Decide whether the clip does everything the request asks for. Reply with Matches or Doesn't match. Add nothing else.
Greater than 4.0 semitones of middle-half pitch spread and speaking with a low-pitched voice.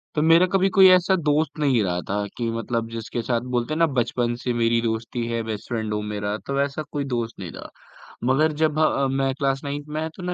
Matches